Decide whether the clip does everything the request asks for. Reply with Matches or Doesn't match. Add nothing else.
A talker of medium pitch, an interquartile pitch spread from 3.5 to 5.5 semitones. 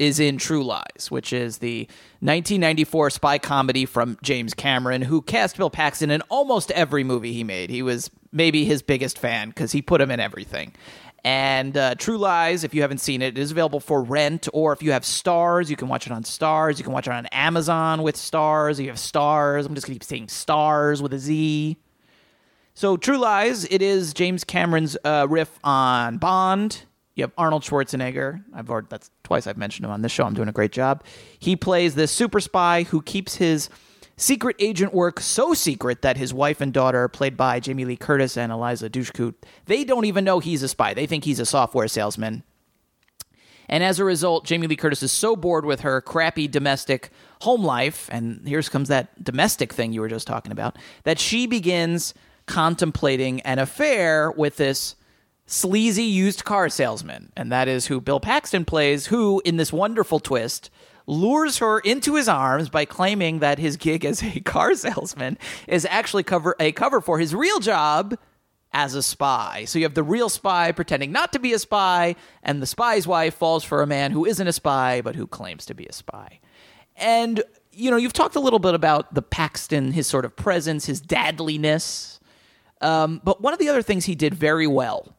Matches